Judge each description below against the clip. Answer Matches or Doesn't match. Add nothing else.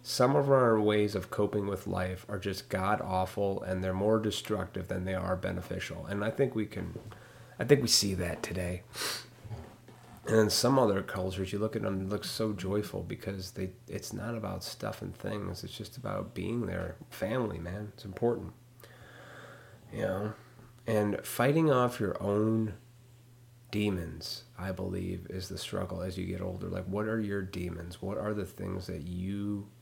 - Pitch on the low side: Matches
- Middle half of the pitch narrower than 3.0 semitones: Doesn't match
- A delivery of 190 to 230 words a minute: Doesn't match